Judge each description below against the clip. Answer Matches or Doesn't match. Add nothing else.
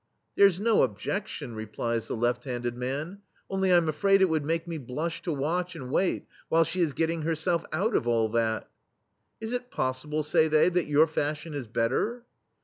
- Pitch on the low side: Doesn't match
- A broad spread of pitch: Matches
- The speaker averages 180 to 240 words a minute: Matches